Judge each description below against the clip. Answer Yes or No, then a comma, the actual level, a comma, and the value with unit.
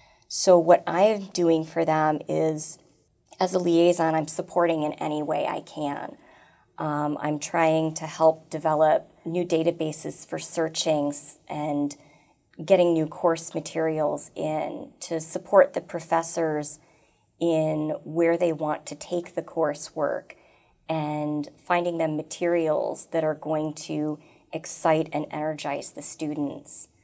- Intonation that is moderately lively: No, narrow, 1.8 semitones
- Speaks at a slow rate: Yes, slow, 130 wpm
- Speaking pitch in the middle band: Yes, medium, 160 Hz